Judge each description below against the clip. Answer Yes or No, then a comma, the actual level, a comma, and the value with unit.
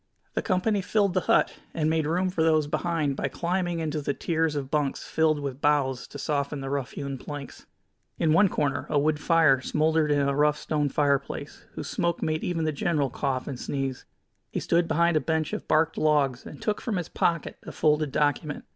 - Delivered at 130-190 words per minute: No, fast, 205 wpm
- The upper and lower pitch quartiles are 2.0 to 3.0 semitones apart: Yes, average, 2.7 semitones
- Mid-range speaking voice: Yes, medium, 150 Hz